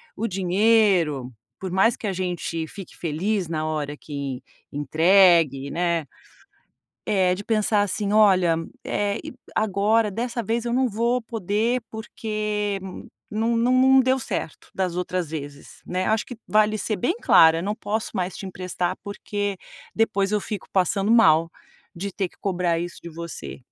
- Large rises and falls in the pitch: No, average, 4.0 semitones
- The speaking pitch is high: Yes, high, 195 Hz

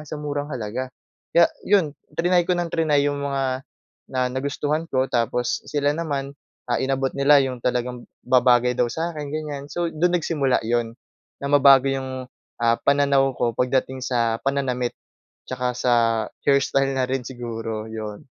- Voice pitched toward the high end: No, low, 135 Hz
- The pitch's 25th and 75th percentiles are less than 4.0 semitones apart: Yes, average, 2.7 semitones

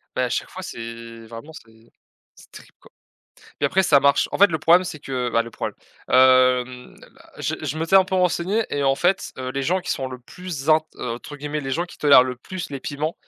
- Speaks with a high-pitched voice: No, medium, 140 Hz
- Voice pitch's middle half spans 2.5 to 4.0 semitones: No, average, 5.2 semitones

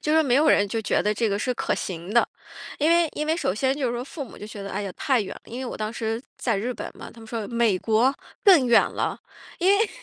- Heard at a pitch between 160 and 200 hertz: No, high, 235 Hz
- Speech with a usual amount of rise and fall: Yes, average, 4.8 semitones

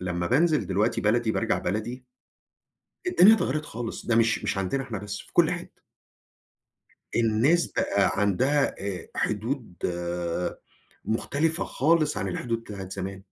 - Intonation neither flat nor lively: No, wide, 5.7 semitones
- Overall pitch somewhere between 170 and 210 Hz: No, low, 115 Hz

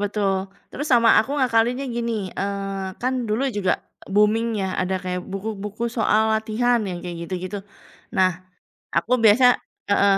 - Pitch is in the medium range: No, high, 210 Hz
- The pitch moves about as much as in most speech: Yes, average, 3.4 semitones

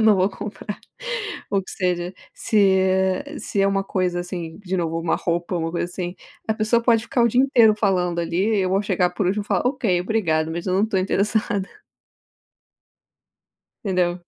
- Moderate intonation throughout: Yes, average, 3.0 semitones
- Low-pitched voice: No, high, 190 Hz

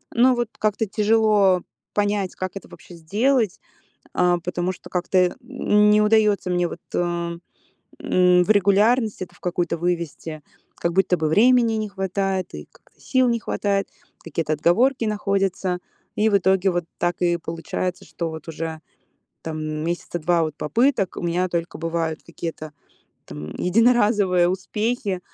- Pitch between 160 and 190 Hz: Yes, medium, 185 Hz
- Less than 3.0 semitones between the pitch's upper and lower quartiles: No, average, 3.5 semitones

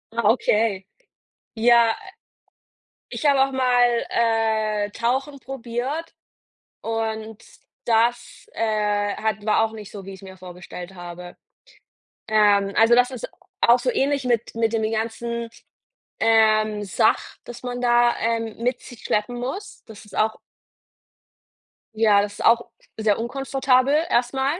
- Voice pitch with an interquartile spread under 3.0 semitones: Yes, narrow, 2.4 semitones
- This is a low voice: No, high, 225 Hz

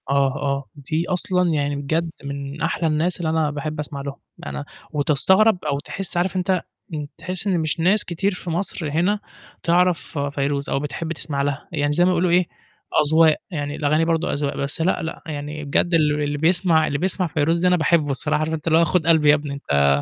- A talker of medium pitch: Yes, medium, 155 Hz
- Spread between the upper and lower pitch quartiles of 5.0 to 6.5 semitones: No, average, 3.1 semitones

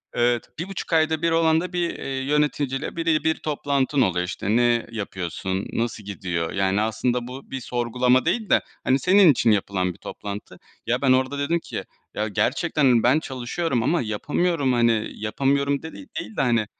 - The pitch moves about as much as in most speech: No, wide, 5.9 semitones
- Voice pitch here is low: Yes, low, 130 Hz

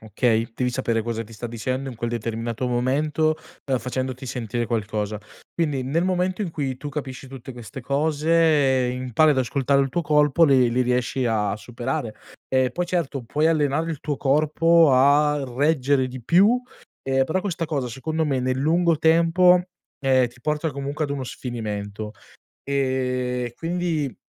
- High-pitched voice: No, low, 135 Hz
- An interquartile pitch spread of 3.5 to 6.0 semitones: Yes, average, 3.9 semitones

